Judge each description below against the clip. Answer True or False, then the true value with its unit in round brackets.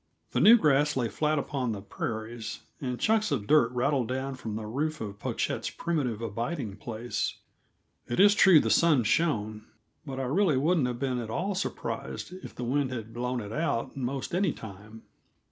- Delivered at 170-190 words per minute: True (180 wpm)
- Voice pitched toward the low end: True (125 Hz)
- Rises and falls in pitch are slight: False (5.3 semitones)